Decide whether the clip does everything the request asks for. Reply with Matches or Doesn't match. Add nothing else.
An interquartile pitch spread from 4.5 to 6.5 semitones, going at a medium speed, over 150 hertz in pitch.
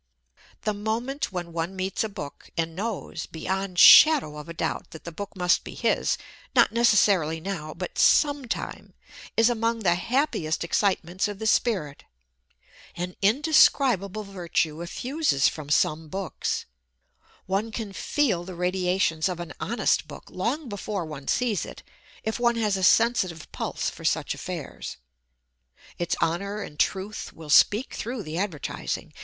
Matches